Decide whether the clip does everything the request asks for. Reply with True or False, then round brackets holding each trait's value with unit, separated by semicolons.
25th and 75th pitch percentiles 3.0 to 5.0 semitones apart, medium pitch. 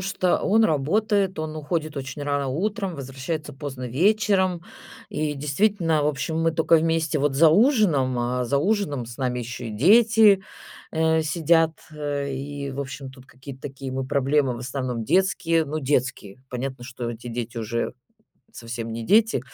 True (4.4 semitones; 145 Hz)